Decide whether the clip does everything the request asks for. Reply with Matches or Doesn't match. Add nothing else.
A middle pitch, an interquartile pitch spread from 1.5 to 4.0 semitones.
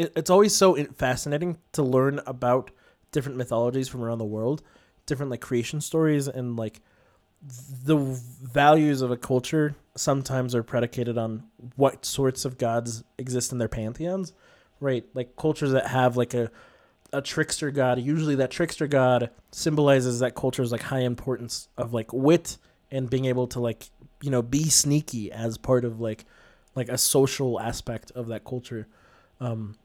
Doesn't match